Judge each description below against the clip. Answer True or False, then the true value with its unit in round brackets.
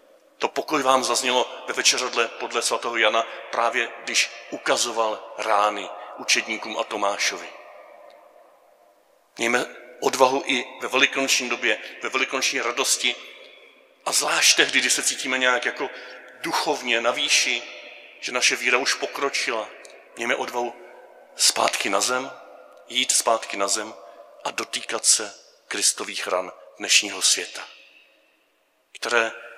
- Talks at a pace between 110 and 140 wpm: True (120 wpm)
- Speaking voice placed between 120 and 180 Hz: True (130 Hz)